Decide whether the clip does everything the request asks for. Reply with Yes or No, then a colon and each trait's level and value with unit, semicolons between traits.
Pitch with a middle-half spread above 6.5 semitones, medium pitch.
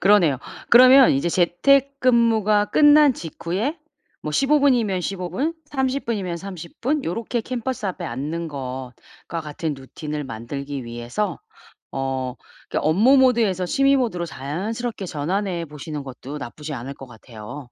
Yes: wide, 8.9 semitones; medium, 180 Hz